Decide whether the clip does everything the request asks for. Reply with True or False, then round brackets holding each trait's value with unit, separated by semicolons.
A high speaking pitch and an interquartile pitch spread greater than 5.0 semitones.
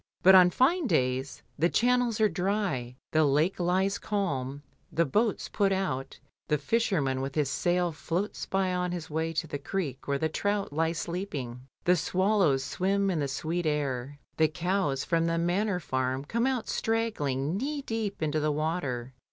False (170 Hz; 5.5 semitones)